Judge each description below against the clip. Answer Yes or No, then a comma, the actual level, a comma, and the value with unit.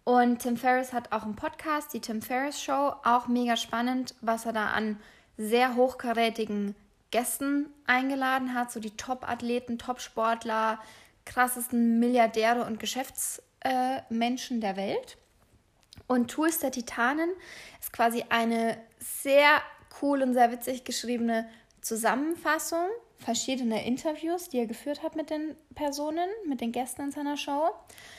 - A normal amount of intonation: Yes, average, 3.7 semitones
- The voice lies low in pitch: No, very high, 250 Hz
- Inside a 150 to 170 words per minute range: No, average, 135 wpm